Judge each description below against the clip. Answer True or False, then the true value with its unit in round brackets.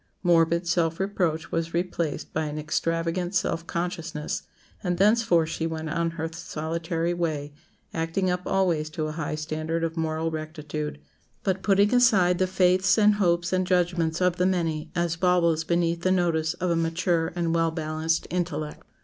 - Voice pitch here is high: False (170 Hz)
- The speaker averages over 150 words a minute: True (165 wpm)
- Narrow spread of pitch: True (1.9 semitones)